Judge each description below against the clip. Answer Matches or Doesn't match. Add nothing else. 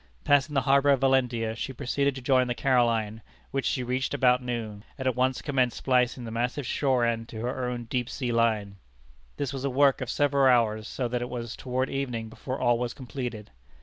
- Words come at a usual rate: Doesn't match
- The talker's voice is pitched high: Doesn't match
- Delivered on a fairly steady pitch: Matches